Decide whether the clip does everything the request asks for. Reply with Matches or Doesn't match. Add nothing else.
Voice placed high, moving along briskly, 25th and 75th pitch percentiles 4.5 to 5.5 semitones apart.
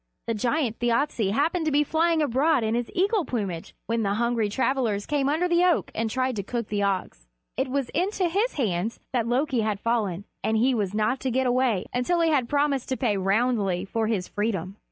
Matches